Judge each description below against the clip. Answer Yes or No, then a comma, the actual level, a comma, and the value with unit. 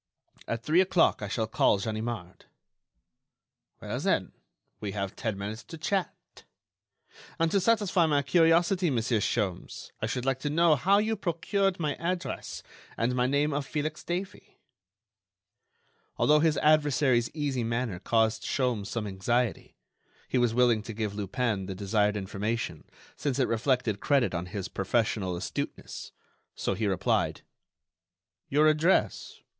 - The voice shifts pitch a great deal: Yes, wide, 6.3 semitones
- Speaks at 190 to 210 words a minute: No, average, 140 wpm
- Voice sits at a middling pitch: No, low, 125 Hz